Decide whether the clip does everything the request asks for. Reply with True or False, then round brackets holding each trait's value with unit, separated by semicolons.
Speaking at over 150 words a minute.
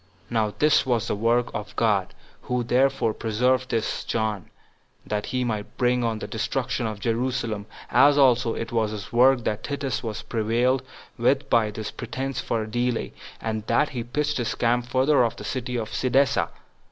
True (175 wpm)